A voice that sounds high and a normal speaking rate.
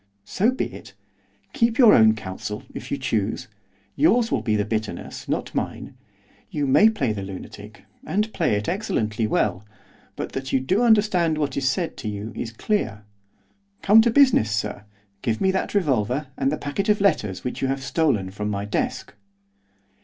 No: low, 135 Hz; average, 175 wpm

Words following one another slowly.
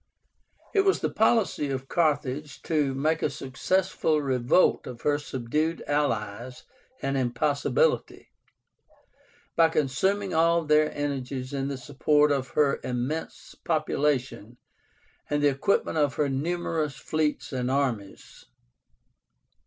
Yes: slow, 115 wpm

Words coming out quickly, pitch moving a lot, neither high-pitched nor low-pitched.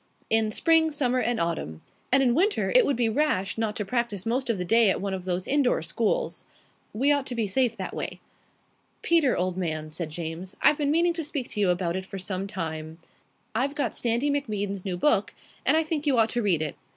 No: fast, 225 wpm; wide, 7.2 semitones; high, 225 Hz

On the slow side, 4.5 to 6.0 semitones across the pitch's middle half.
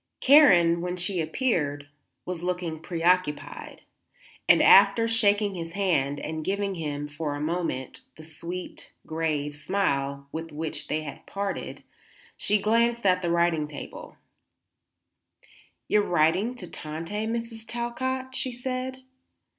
Yes: slow, 130 wpm; average, 5.1 semitones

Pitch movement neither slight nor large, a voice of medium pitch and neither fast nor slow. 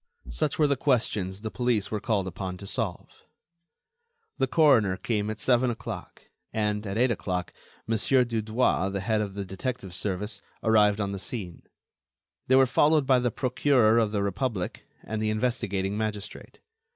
No: average, 3.8 semitones; low, 110 Hz; average, 165 wpm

